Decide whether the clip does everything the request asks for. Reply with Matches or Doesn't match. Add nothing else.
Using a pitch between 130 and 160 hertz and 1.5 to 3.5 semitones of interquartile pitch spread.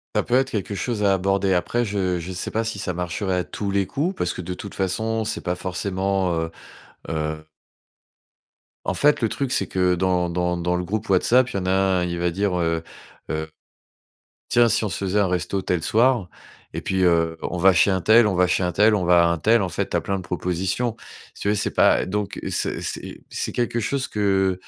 Doesn't match